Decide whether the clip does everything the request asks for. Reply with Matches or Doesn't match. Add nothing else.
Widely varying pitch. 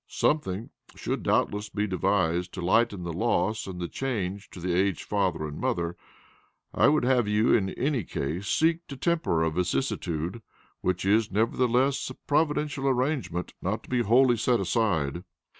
Matches